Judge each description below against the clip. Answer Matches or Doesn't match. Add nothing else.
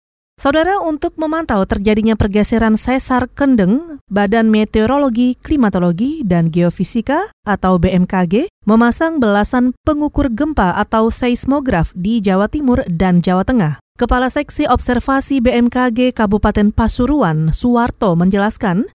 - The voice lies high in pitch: Matches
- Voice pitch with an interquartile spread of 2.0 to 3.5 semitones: Doesn't match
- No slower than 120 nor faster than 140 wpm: Doesn't match